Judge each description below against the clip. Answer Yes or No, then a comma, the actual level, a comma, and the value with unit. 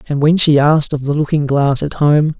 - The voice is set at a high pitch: No, medium, 145 Hz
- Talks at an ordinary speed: No, fast, 250 wpm